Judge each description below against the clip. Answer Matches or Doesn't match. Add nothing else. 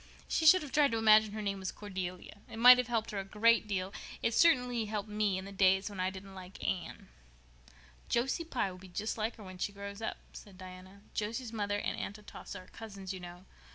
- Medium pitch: Doesn't match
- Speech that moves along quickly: Matches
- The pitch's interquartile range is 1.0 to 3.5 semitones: Matches